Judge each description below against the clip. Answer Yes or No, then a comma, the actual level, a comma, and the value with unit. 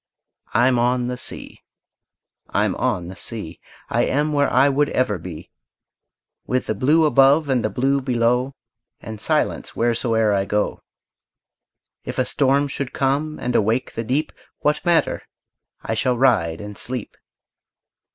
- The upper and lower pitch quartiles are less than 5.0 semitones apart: Yes, average, 3.8 semitones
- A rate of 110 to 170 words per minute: Yes, average, 145 wpm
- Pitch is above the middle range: No, low, 125 Hz